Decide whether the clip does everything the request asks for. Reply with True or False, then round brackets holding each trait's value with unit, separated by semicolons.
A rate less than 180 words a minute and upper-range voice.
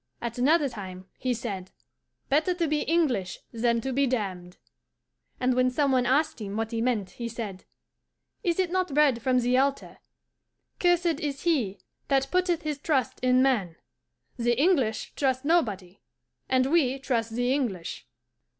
True (160 wpm; 255 Hz)